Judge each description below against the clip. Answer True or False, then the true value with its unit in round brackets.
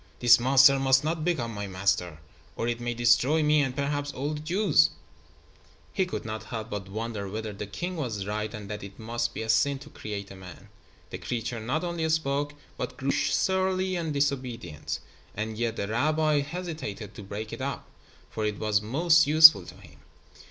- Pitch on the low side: True (120 Hz)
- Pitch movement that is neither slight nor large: False (6.0 semitones)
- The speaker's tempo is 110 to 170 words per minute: False (190 wpm)